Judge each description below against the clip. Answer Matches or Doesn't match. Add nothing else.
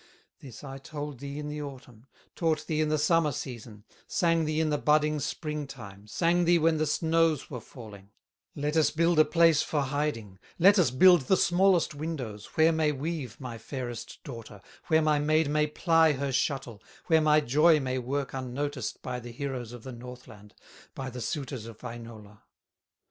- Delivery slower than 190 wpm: Matches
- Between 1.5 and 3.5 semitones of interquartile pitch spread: Doesn't match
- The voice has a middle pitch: Matches